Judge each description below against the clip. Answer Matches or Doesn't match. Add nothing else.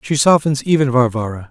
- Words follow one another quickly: Doesn't match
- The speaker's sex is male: Matches